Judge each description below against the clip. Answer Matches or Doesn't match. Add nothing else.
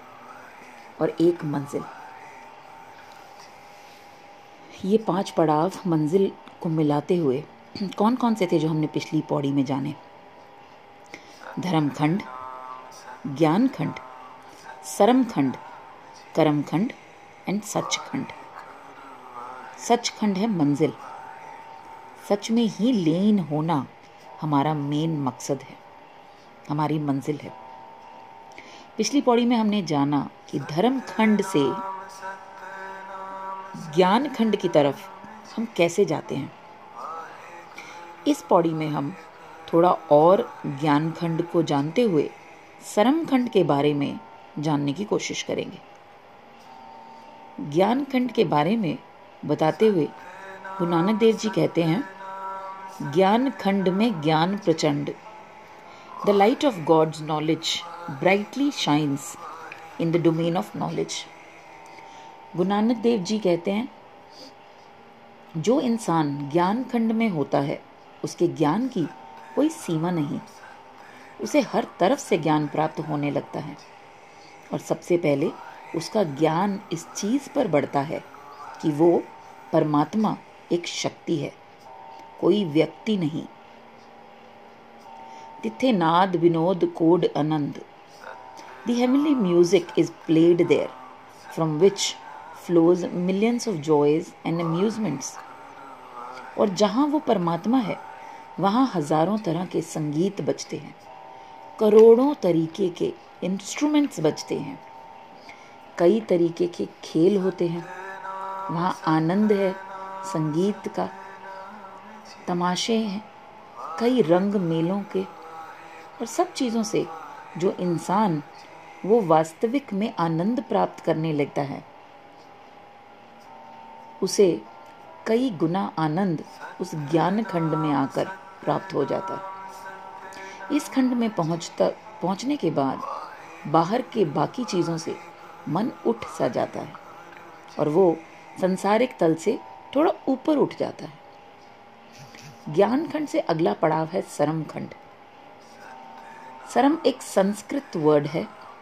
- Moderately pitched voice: Matches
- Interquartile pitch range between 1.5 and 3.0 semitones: Doesn't match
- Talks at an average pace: Doesn't match